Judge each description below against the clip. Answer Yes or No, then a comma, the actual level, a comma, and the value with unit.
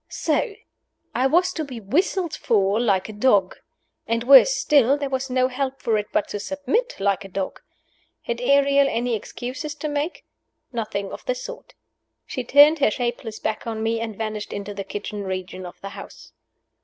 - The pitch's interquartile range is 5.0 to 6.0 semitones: Yes, average, 5.3 semitones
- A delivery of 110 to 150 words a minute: No, average, 180 wpm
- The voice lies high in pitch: Yes, high, 240 Hz